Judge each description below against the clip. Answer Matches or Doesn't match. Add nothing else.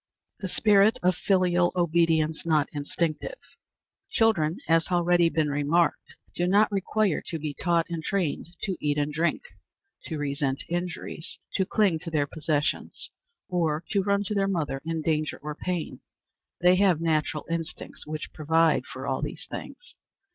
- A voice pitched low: Doesn't match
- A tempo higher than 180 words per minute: Doesn't match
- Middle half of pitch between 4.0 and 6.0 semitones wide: Doesn't match